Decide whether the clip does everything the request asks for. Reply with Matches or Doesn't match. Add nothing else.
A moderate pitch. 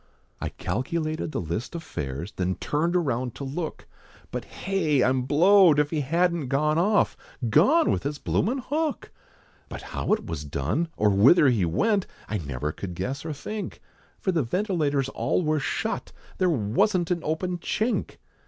Matches